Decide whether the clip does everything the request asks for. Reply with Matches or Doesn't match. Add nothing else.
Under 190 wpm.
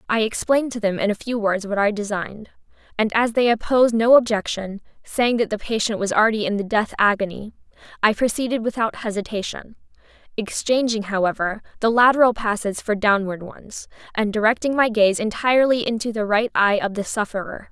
Matches